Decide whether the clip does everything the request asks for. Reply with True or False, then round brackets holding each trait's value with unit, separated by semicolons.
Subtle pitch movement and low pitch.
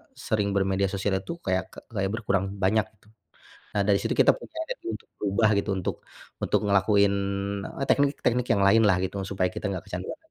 True (2.3 semitones; 100 Hz)